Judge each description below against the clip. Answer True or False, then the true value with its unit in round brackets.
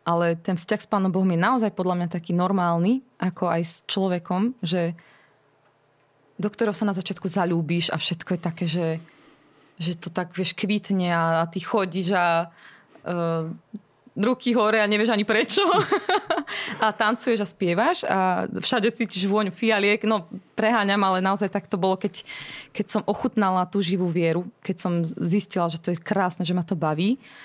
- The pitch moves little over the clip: False (3.5 semitones)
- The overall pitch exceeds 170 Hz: True (190 Hz)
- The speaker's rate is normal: False (175 wpm)